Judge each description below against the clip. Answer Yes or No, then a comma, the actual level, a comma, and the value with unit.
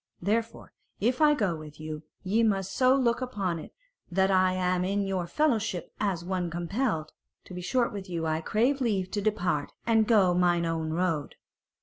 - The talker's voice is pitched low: No, high, 190 Hz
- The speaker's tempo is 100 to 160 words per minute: No, average, 185 wpm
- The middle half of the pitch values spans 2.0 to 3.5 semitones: No, average, 4.4 semitones